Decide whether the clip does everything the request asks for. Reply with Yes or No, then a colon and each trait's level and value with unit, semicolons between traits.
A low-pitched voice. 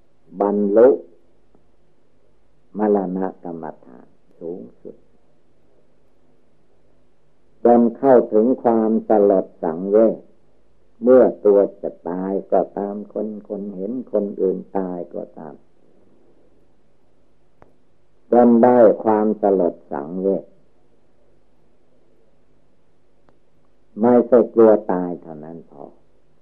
Yes: low, 100 Hz